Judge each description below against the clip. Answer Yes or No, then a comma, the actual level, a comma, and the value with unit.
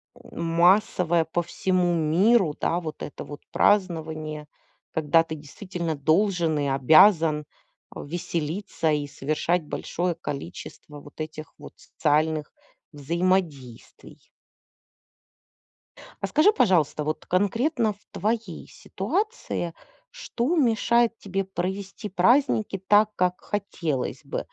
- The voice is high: No, medium, 175 Hz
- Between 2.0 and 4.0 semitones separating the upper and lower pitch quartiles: No, average, 4.6 semitones